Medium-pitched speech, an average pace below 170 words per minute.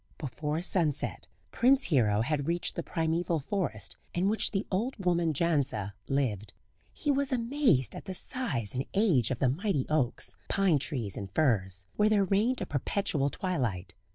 Yes: medium, 155 Hz; average, 160 wpm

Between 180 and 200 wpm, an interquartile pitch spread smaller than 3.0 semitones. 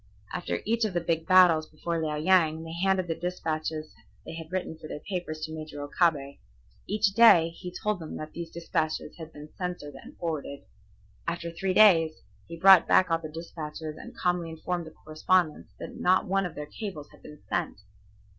Yes: average, 185 wpm; narrow, 2.5 semitones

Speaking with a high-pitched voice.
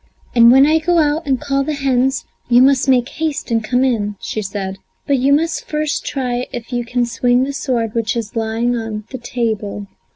Yes: high, 245 Hz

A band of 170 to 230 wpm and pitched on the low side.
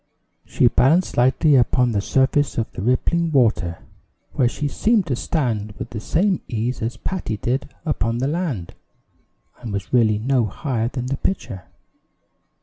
No: average, 155 wpm; low, 125 Hz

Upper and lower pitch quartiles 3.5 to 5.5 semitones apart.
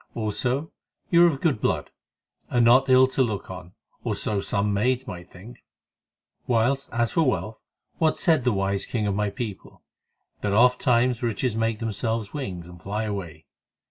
Yes: average, 4.1 semitones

